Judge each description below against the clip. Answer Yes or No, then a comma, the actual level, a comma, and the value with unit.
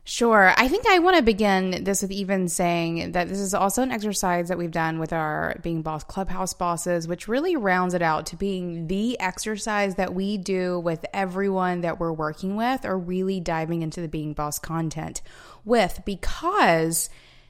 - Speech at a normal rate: Yes, average, 185 wpm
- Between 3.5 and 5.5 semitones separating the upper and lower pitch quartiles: No, average, 2.8 semitones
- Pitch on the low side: No, medium, 185 Hz